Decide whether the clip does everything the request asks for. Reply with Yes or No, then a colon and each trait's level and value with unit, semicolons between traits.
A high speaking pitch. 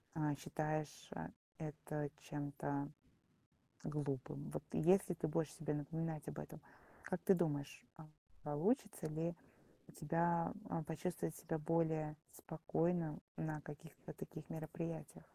No: medium, 155 Hz